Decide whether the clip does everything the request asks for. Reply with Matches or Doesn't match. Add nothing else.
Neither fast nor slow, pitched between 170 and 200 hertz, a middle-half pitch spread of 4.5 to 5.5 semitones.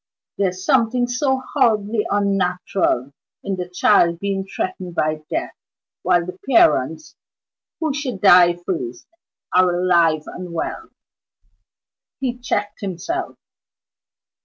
Doesn't match